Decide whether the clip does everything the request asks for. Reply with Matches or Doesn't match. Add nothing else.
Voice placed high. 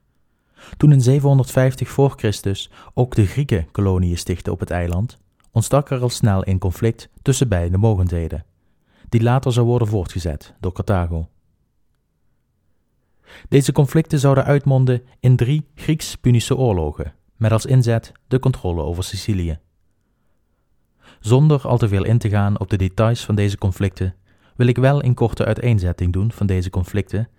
Doesn't match